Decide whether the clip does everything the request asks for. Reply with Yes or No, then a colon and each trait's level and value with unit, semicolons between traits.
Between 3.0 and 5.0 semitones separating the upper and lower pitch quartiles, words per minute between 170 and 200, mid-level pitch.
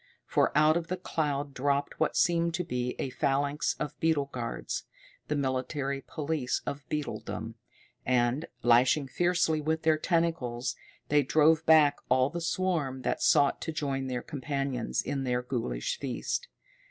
No: average, 3.4 semitones; average, 150 wpm; medium, 145 Hz